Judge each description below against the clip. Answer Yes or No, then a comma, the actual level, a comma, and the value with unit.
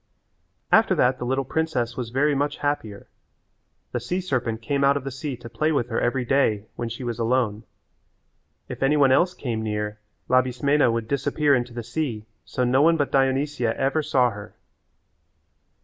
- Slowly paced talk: No, average, 180 wpm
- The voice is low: Yes, low, 130 Hz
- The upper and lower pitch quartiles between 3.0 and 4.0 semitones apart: Yes, average, 3.4 semitones